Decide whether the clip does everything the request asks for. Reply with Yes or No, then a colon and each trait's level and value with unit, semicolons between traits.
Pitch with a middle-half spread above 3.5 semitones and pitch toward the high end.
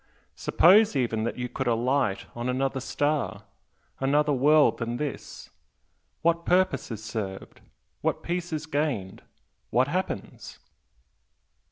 No: average, 4.7 semitones; low, 135 Hz